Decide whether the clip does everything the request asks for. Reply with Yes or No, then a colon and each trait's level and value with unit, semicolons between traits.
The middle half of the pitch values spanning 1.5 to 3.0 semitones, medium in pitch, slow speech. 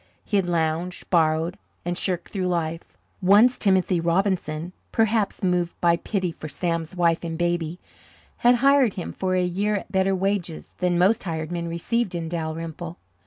No: narrow, 2.6 semitones; medium, 175 Hz; average, 165 wpm